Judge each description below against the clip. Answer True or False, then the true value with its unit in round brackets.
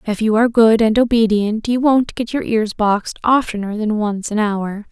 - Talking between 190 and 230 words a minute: True (205 wpm)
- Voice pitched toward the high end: True (220 Hz)